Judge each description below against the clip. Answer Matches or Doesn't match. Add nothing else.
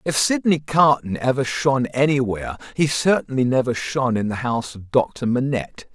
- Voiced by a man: Matches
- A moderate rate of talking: Matches